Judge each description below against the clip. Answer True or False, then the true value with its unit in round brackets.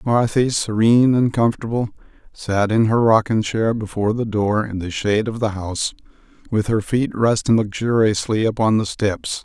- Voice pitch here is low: True (110 Hz)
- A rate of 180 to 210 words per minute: False (165 wpm)